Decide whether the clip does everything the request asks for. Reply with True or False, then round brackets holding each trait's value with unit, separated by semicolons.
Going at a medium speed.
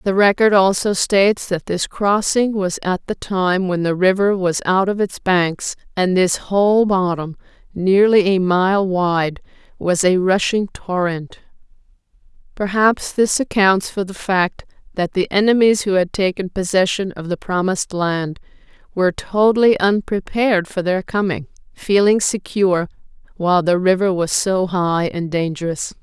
True (150 wpm)